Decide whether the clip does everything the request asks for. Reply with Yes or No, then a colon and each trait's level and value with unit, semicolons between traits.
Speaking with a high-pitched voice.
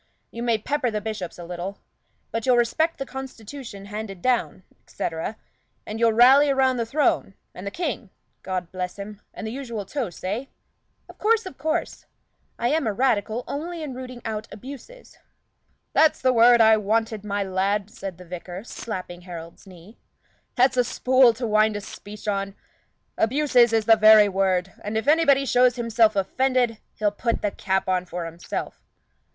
Yes: high, 220 Hz